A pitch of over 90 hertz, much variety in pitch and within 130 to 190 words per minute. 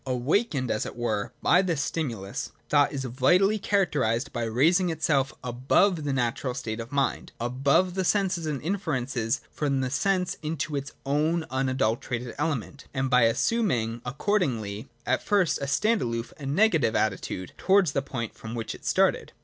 Yes: low, 135 Hz; wide, 5.7 semitones; average, 160 wpm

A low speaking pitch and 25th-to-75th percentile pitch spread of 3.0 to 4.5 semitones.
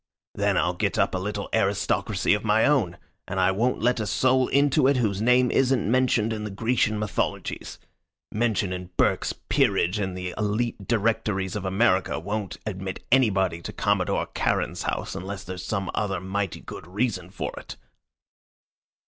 Yes: low, 105 Hz; average, 3.3 semitones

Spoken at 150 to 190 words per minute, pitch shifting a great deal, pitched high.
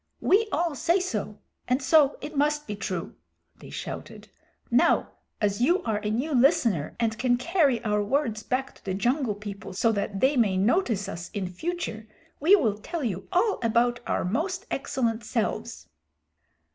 Yes: average, 170 wpm; wide, 6.1 semitones; high, 240 Hz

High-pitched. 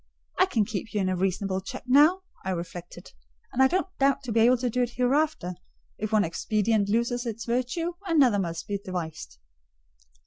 Yes: high, 225 Hz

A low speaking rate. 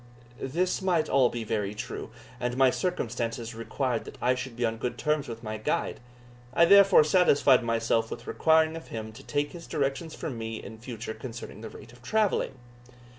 No: average, 185 wpm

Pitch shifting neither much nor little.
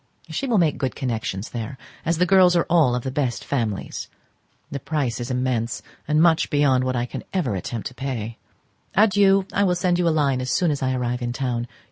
No: wide, 5.7 semitones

